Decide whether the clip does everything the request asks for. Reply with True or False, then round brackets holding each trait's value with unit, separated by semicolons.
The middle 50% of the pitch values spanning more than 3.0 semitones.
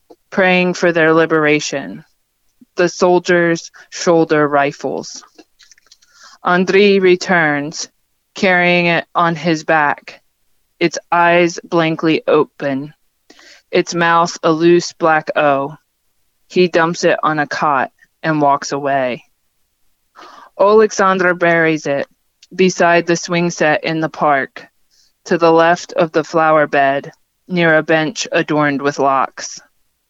False (2.5 semitones)